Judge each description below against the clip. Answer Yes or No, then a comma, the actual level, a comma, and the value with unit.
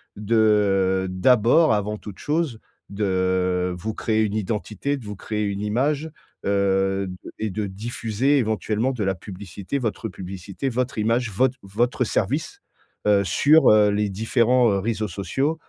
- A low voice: Yes, low, 105 Hz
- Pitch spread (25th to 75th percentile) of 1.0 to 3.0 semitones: No, average, 3.5 semitones